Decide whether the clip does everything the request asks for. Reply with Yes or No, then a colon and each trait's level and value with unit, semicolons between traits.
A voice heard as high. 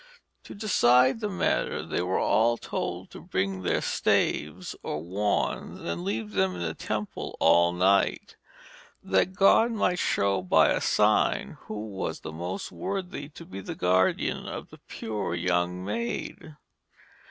No: low, 100 Hz